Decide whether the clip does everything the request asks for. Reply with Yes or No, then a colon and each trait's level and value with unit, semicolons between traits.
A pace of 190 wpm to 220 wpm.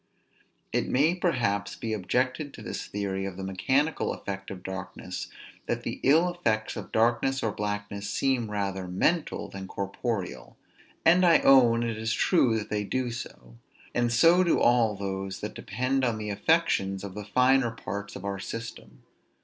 No: average, 165 wpm